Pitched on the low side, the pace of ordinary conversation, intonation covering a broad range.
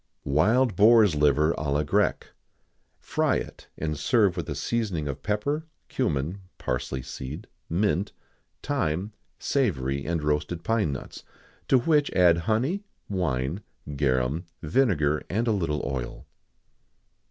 No: very low, 85 Hz; slow, 130 wpm; wide, 6.9 semitones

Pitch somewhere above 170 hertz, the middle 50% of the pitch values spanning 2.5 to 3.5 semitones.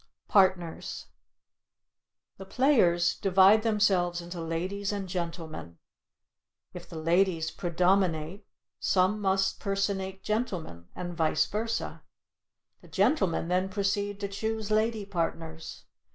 Yes: high, 190 Hz; average, 2.9 semitones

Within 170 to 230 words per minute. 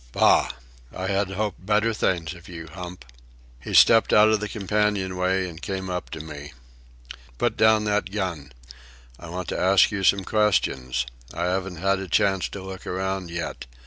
Yes: average, 175 wpm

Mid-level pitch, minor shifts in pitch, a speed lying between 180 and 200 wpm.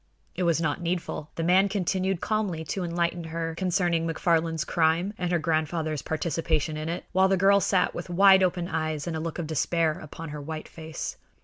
Yes: medium, 170 Hz; narrow, 2.3 semitones; average, 195 wpm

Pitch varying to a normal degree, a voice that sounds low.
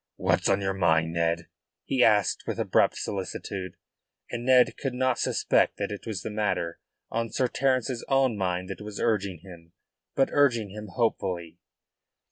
Yes: average, 4.7 semitones; low, 105 Hz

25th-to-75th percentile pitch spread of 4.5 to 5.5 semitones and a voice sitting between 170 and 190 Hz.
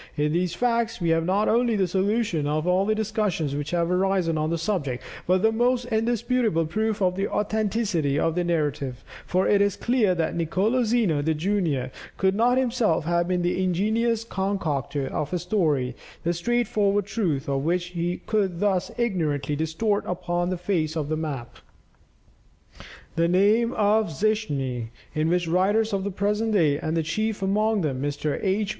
Yes: average, 5.0 semitones; medium, 185 Hz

